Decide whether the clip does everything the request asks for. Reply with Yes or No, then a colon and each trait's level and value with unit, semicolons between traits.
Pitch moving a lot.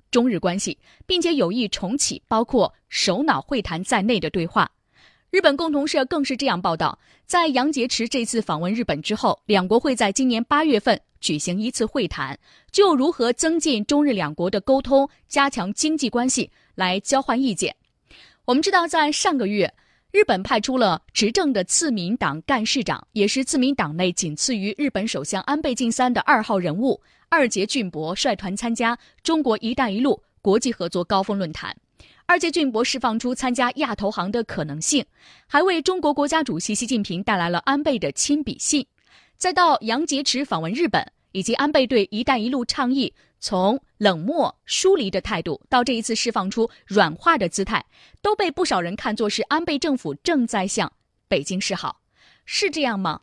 Yes: wide, 5.9 semitones